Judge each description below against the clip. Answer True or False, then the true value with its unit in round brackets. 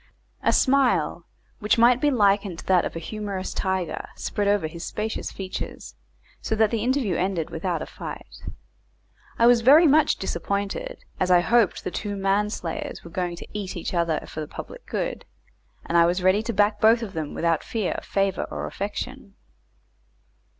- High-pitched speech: True (200 Hz)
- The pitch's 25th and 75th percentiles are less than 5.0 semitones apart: True (4.1 semitones)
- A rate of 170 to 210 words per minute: True (180 wpm)